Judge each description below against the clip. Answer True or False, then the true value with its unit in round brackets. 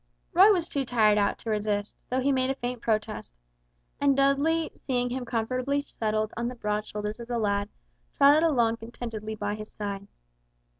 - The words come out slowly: False (180 wpm)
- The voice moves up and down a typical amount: True (4.0 semitones)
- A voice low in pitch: False (235 Hz)